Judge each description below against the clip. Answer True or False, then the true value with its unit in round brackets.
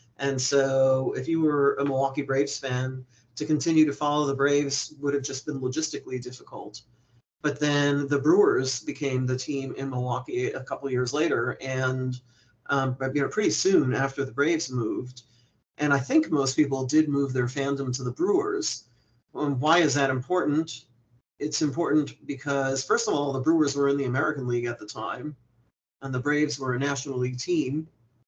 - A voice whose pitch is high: False (140 Hz)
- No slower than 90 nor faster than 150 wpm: False (180 wpm)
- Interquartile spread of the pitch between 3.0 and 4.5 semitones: False (2.6 semitones)